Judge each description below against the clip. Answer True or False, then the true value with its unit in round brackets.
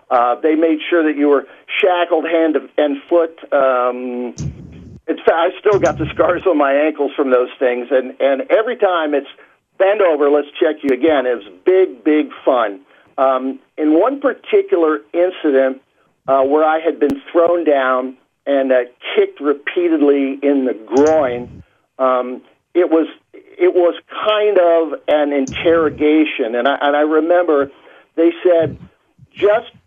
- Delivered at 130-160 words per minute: True (155 wpm)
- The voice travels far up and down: False (4.1 semitones)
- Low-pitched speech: False (150 Hz)